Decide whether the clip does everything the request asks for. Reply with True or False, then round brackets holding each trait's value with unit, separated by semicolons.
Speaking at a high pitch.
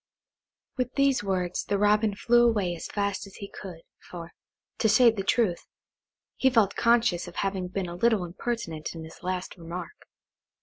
True (195 Hz)